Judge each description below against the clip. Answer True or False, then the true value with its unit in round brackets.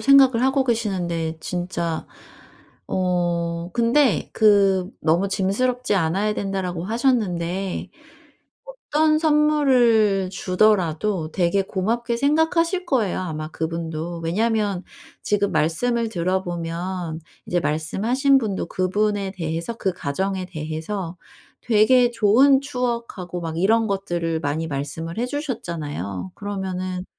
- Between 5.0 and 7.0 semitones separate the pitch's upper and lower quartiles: True (5.5 semitones)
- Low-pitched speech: False (190 Hz)